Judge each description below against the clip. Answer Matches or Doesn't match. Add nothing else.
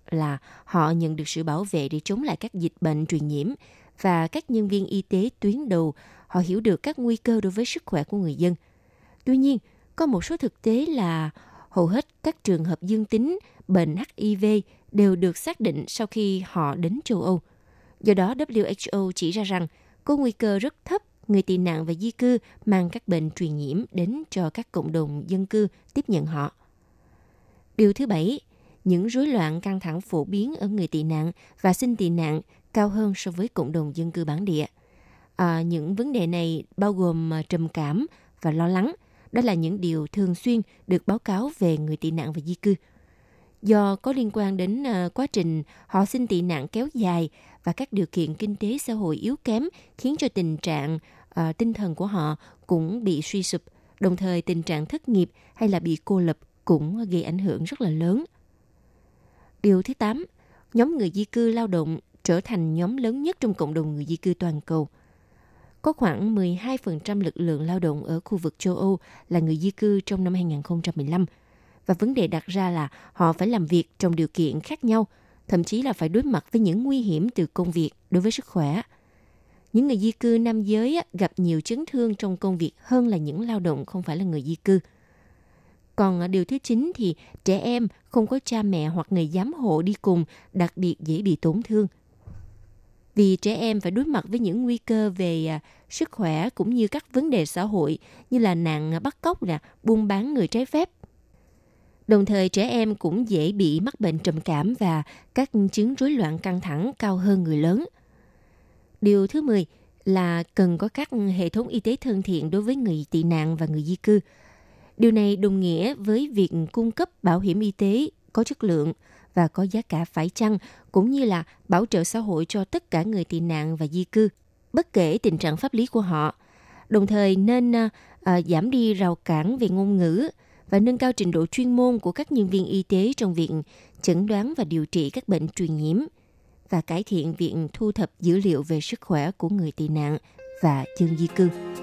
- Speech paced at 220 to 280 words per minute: Doesn't match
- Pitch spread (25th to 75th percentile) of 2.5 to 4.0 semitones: Doesn't match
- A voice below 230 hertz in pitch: Matches